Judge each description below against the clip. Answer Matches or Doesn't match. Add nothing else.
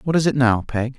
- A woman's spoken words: Doesn't match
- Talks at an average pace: Doesn't match